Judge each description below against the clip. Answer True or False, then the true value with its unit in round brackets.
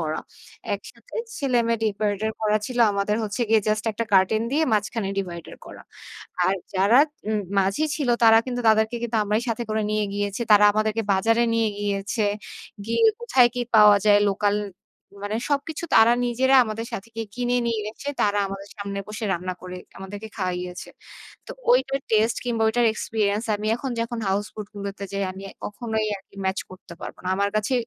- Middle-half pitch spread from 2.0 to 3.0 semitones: True (2.5 semitones)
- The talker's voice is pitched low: False (215 Hz)